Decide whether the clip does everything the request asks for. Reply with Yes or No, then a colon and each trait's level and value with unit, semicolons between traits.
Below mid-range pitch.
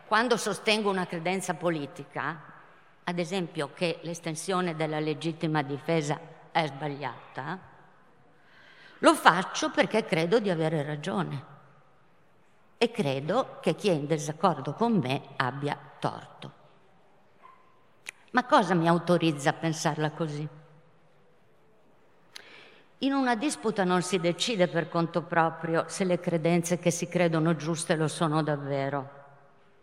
No: medium, 170 Hz